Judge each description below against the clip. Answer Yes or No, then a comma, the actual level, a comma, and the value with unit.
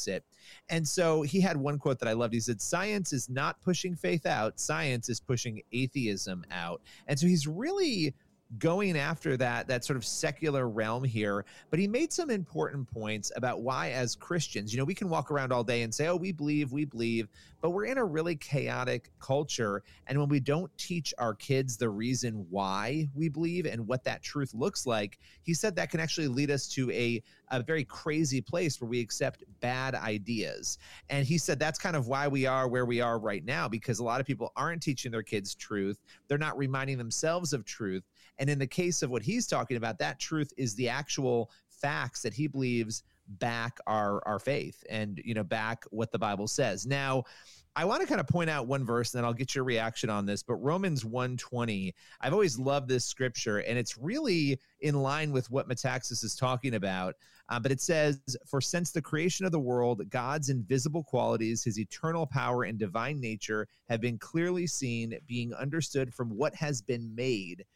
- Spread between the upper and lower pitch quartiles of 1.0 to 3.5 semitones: No, average, 4.6 semitones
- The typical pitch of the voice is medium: No, low, 130 Hz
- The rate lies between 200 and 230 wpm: Yes, fast, 205 wpm